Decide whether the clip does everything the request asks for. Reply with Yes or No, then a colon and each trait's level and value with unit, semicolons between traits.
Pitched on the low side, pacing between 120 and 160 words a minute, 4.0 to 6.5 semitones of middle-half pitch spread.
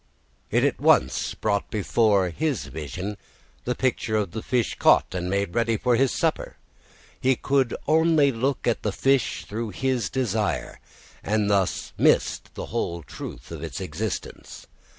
Yes: low, 110 Hz; average, 150 wpm; average, 4.7 semitones